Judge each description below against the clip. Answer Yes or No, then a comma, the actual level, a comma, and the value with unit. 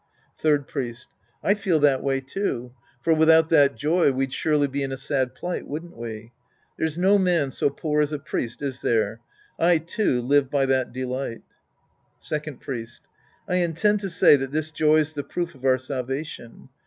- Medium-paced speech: Yes, average, 180 wpm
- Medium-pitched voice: Yes, medium, 145 Hz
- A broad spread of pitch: No, average, 3.6 semitones